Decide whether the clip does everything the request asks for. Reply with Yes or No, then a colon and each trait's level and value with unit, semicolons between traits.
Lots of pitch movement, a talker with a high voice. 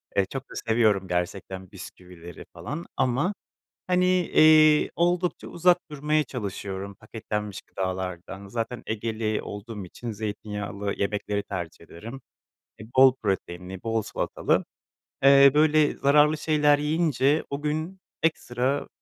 No: wide, 7.1 semitones; low, 115 Hz